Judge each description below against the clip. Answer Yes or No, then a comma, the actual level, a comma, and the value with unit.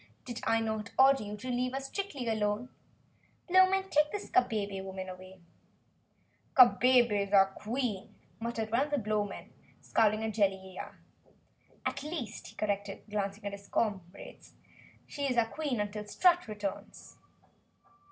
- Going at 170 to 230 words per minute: No, average, 140 wpm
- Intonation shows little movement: No, average, 4.2 semitones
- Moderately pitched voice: No, high, 220 Hz